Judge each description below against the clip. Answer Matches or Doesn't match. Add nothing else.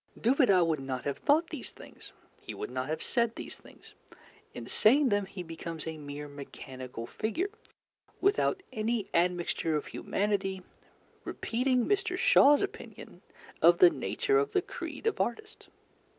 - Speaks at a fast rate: Doesn't match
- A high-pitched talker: Matches